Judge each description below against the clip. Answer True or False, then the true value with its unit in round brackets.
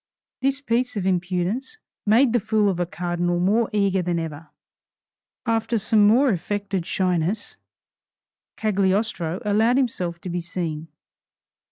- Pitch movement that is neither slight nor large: True (4.2 semitones)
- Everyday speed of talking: False (130 wpm)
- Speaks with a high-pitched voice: True (195 Hz)